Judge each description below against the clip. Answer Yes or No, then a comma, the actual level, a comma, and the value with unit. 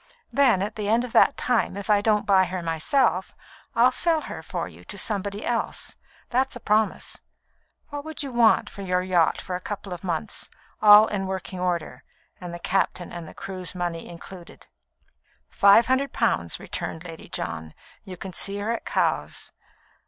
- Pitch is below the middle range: No, high, 200 Hz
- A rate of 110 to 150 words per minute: No, average, 175 wpm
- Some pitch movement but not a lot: Yes, average, 4.1 semitones